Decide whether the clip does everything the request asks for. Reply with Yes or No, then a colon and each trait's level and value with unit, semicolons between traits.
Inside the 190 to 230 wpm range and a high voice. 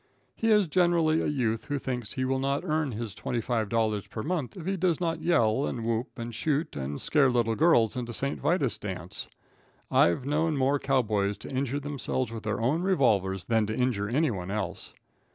No: average, 200 wpm; low, 130 Hz